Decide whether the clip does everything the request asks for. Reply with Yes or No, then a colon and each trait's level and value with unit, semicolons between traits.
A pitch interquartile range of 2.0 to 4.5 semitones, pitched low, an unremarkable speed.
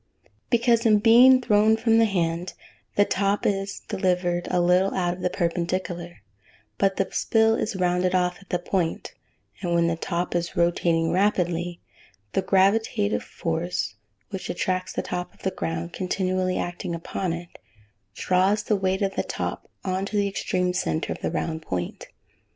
No: narrow, 2.4 semitones; medium, 185 Hz; average, 170 wpm